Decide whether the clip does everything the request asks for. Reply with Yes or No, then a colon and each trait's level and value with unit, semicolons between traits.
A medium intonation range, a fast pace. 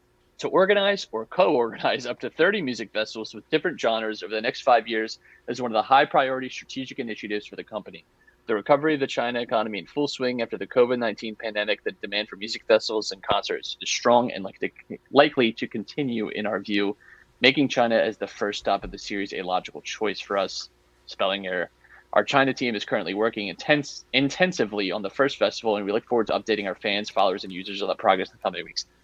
Yes: average, 4.2 semitones; fast, 215 wpm